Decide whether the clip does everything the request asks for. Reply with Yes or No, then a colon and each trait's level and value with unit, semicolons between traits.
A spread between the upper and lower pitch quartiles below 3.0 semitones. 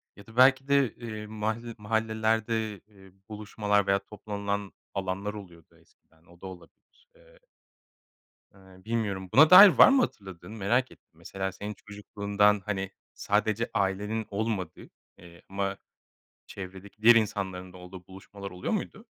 Yes: narrow, 2.5 semitones